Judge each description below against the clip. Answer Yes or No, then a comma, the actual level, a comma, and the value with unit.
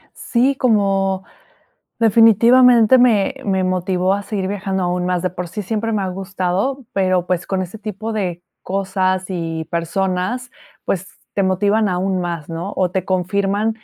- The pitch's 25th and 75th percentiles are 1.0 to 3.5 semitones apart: Yes, average, 2.7 semitones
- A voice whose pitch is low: No, high, 190 Hz